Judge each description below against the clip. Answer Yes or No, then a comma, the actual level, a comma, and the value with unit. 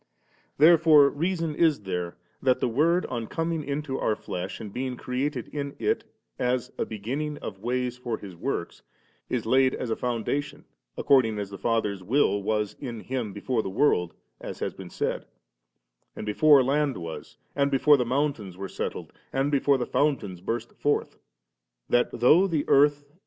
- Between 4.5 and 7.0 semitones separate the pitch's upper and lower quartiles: Yes, average, 5.1 semitones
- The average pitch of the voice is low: Yes, low, 130 Hz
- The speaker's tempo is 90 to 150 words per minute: No, average, 175 wpm